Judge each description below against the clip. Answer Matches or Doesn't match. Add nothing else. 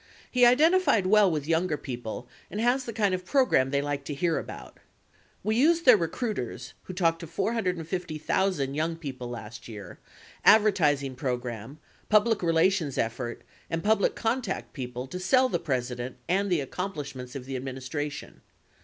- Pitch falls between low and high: Matches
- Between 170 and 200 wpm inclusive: Doesn't match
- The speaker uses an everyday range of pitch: Doesn't match